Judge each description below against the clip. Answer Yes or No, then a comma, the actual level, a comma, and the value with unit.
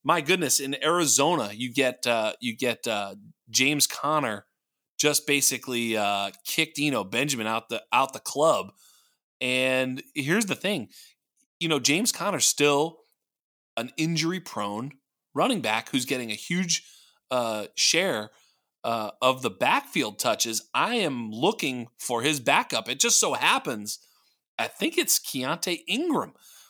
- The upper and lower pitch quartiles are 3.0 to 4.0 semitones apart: No, average, 5.2 semitones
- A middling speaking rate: Yes, average, 145 wpm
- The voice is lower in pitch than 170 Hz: Yes, low, 135 Hz